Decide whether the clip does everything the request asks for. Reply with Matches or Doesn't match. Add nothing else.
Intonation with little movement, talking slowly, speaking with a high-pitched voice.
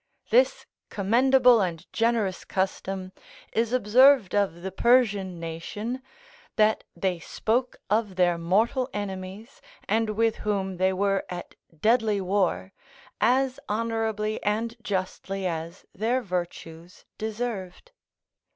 Doesn't match